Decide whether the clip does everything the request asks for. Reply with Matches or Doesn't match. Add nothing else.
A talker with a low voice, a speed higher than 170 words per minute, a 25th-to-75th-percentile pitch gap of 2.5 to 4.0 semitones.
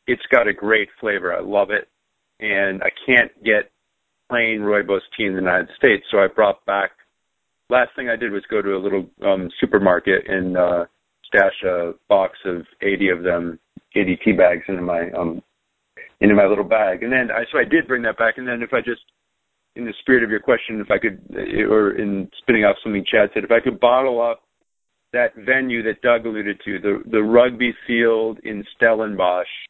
Matches